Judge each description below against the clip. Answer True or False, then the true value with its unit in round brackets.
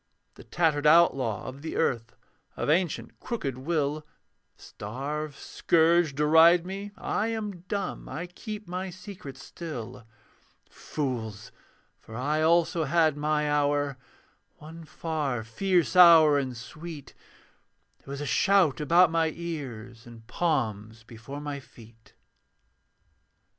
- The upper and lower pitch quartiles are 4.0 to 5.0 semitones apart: True (4.6 semitones)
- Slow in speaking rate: True (120 wpm)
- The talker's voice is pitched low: False (150 Hz)